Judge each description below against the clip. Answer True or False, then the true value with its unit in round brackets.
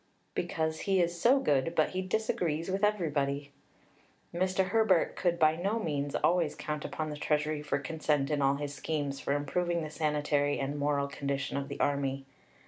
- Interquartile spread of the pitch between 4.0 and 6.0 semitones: False (3.3 semitones)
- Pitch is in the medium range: True (150 Hz)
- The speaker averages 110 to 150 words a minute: False (175 wpm)